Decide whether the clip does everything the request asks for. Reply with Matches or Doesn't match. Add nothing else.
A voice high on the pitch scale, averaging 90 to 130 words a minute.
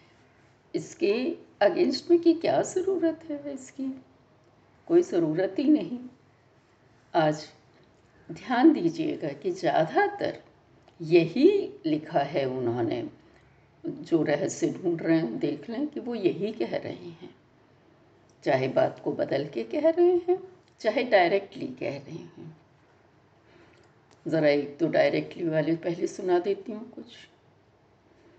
Matches